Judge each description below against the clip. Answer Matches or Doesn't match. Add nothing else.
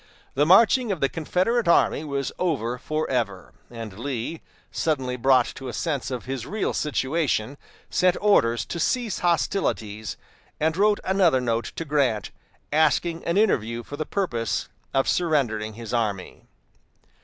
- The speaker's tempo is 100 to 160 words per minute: Matches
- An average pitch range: Doesn't match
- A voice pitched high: Doesn't match